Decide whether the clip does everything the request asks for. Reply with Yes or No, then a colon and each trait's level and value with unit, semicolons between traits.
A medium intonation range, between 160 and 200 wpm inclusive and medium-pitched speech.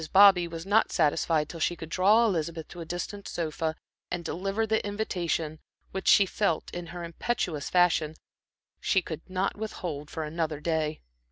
Yes: average, 3.3 semitones; average, 165 wpm; medium, 170 Hz